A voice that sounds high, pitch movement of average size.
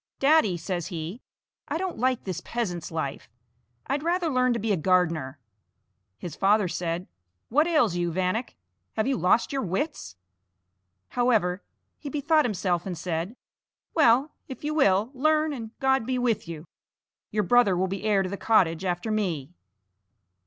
No: high, 210 Hz; wide, 6.7 semitones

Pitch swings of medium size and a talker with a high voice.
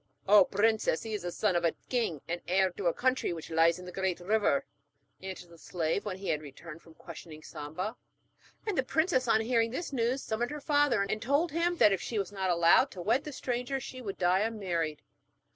No: wide, 6.1 semitones; high, 200 Hz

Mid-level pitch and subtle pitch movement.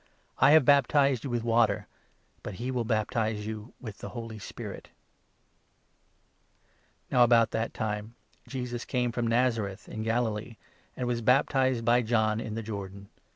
No: low, 115 Hz; narrow, 2.2 semitones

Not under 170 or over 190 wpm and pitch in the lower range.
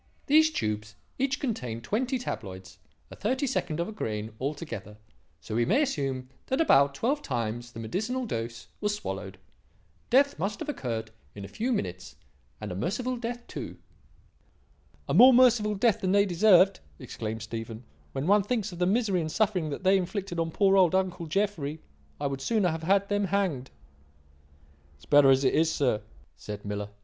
No: average, 175 wpm; medium, 180 Hz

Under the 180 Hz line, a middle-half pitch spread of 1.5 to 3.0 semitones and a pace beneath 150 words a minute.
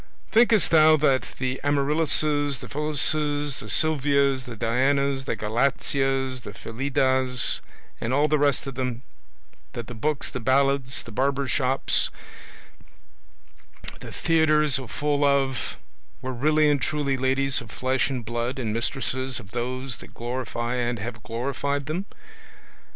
Yes: low, 135 Hz; narrow, 2.4 semitones; average, 140 wpm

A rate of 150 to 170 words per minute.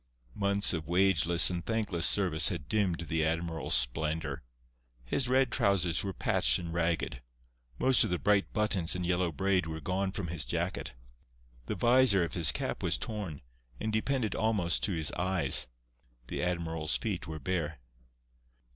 Yes: average, 155 wpm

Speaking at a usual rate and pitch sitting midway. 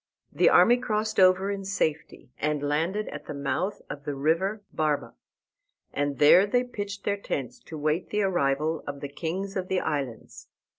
Yes: average, 170 wpm; medium, 165 Hz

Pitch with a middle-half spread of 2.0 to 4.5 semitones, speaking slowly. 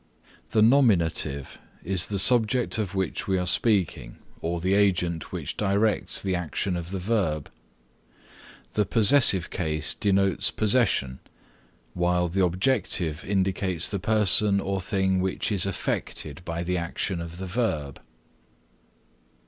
Yes: average, 3.0 semitones; slow, 130 wpm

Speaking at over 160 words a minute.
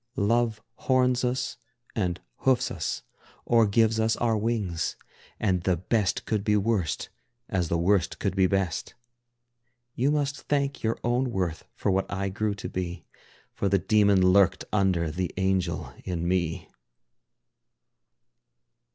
No: average, 140 wpm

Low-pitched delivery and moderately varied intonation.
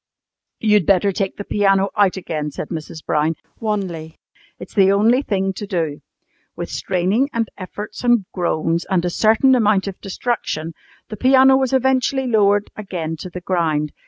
No: high, 195 Hz; average, 4.2 semitones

